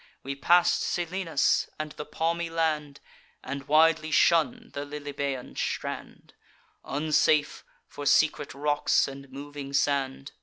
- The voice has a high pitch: No, medium, 150 Hz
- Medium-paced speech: No, slow, 115 wpm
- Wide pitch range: No, narrow, 2.5 semitones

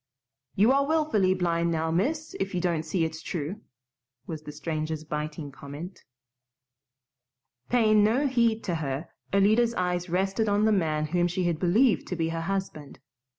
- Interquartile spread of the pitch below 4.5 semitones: No, average, 4.9 semitones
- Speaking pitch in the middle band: Yes, medium, 180 Hz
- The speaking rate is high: No, average, 160 wpm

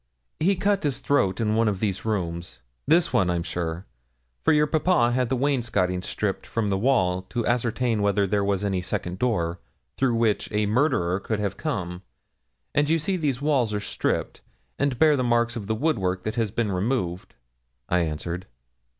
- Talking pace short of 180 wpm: No, average, 185 wpm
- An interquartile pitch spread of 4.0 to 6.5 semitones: Yes, wide, 5.6 semitones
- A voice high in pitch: No, low, 110 Hz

